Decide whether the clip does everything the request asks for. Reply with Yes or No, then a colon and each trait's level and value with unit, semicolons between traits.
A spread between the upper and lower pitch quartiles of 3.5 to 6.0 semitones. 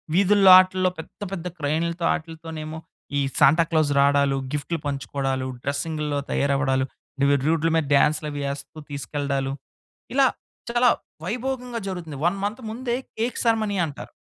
Yes: average, 5.1 semitones